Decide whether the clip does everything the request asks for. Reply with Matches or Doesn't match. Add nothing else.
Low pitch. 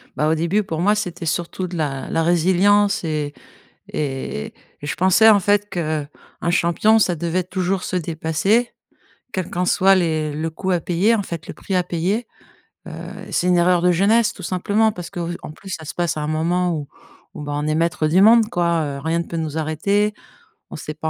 Doesn't match